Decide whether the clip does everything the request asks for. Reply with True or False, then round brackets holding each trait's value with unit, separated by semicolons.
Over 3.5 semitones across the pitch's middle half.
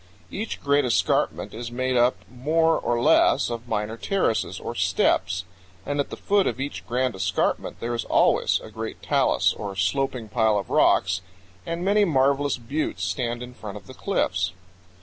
True (4.4 semitones)